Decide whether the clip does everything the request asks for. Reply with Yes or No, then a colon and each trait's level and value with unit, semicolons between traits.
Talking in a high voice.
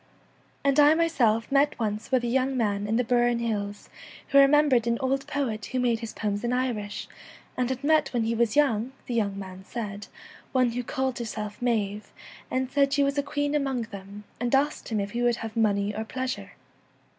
Yes: high, 240 Hz